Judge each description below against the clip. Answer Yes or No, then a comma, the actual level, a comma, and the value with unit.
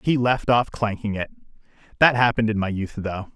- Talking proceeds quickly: No, average, 195 wpm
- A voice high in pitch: No, low, 110 Hz